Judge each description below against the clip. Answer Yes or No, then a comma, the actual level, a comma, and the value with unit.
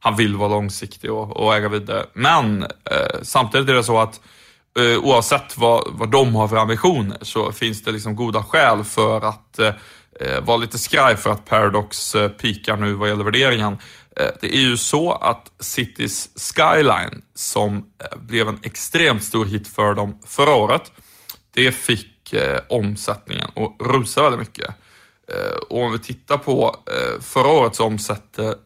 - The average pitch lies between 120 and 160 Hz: No, low, 110 Hz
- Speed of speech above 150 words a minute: Yes, average, 170 wpm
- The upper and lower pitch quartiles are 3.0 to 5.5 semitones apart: No, narrow, 2.5 semitones